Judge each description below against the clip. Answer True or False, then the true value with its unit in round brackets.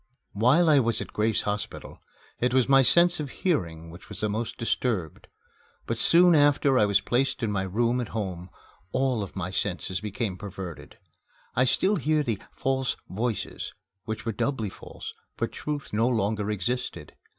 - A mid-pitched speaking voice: False (115 Hz)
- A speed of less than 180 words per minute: True (170 wpm)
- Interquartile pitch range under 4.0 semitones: False (4.6 semitones)